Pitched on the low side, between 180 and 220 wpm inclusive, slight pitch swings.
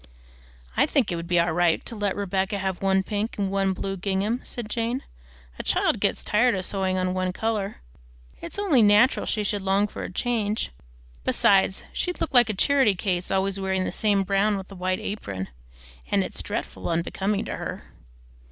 No: high, 195 Hz; average, 190 wpm; narrow, 2.2 semitones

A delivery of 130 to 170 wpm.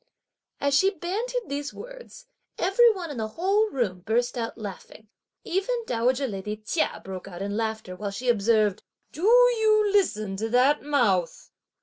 Yes: average, 160 wpm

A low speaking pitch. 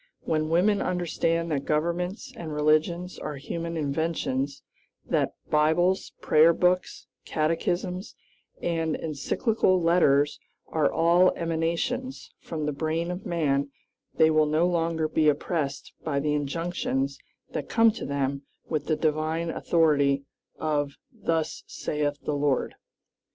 No: medium, 160 Hz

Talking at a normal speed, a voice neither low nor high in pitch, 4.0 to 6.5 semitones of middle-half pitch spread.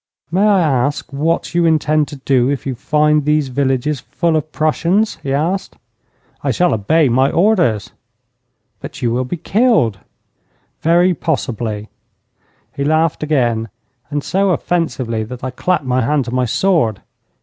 Yes: average, 150 wpm; medium, 150 Hz; average, 4.8 semitones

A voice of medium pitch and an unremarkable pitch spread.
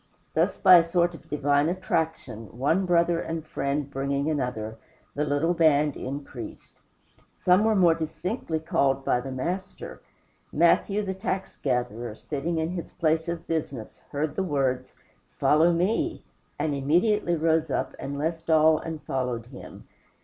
Yes: medium, 155 Hz; average, 3.7 semitones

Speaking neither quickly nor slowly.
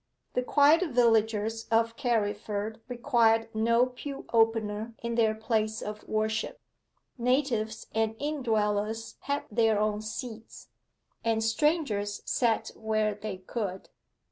No: slow, 115 wpm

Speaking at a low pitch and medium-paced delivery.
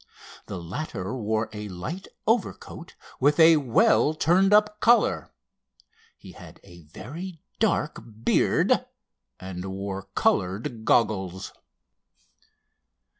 No: low, 115 Hz; slow, 100 wpm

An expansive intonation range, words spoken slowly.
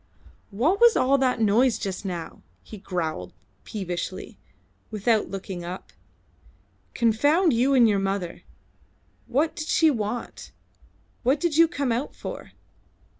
Yes: wide, 6.3 semitones; slow, 125 wpm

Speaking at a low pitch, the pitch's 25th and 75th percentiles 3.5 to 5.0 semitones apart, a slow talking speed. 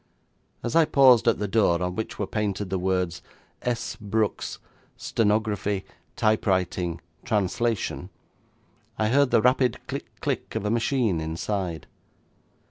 Yes: low, 105 Hz; average, 3.8 semitones; slow, 130 wpm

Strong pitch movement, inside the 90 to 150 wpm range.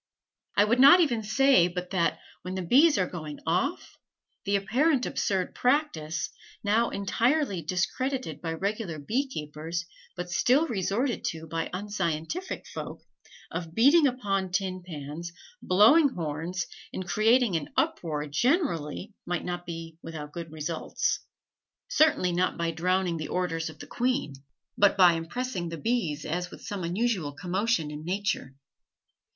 Yes: wide, 6.1 semitones; average, 145 wpm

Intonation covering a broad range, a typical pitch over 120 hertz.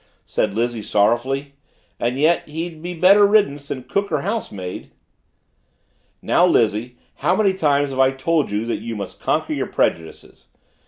Yes: wide, 6.6 semitones; medium, 140 Hz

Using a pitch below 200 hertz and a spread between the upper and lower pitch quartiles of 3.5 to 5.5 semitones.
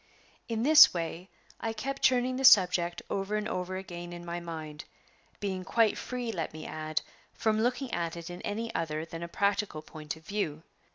Yes: medium, 185 Hz; average, 5.1 semitones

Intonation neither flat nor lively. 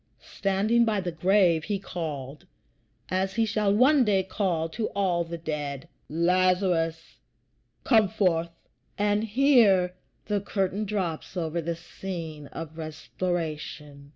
Yes: average, 3.9 semitones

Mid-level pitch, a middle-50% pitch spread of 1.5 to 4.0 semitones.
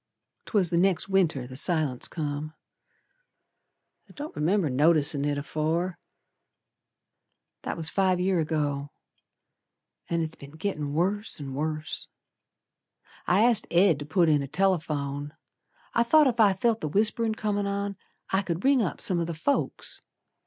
No: medium, 170 Hz; average, 4.8 semitones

